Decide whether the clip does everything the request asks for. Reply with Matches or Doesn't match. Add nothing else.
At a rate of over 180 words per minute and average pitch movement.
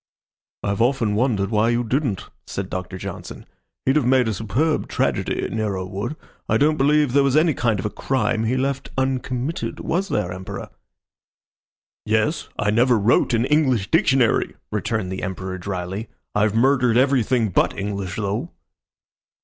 Doesn't match